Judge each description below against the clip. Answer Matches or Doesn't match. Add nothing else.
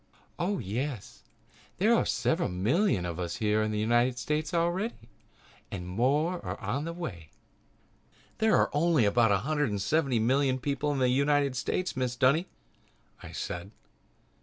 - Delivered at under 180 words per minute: Matches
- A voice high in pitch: Doesn't match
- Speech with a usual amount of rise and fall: Doesn't match